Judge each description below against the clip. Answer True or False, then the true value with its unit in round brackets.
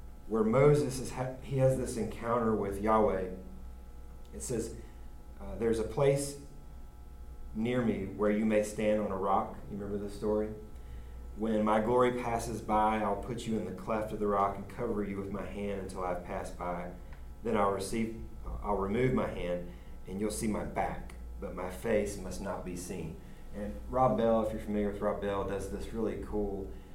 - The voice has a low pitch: True (100 Hz)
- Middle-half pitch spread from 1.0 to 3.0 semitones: False (3.8 semitones)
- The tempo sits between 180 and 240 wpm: True (185 wpm)